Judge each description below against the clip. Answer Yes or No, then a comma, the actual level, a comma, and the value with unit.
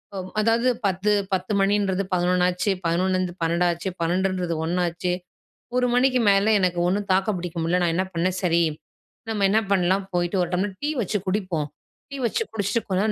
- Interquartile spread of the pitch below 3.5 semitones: Yes, narrow, 2.4 semitones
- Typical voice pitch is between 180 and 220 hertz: Yes, medium, 185 Hz